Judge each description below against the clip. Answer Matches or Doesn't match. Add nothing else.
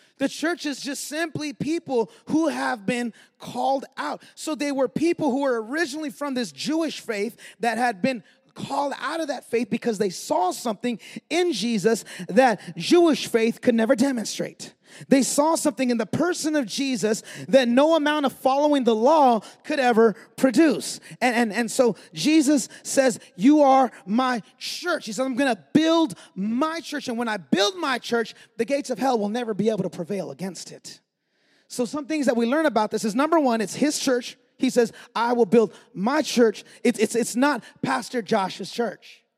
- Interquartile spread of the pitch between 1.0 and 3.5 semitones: Doesn't match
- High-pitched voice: Matches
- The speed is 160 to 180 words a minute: Doesn't match